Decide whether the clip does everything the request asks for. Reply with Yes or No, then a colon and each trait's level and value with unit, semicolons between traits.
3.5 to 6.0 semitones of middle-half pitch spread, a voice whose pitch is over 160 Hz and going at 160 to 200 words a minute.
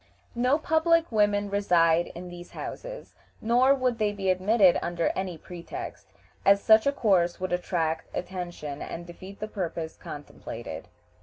No: average, 4.3 semitones; high, 190 Hz; average, 145 wpm